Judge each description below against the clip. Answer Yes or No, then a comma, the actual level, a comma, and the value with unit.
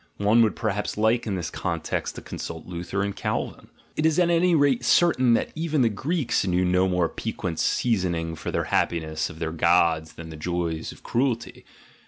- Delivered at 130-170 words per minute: No, average, 190 wpm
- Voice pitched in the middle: No, very low, 95 Hz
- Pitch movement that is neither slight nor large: No, wide, 6.5 semitones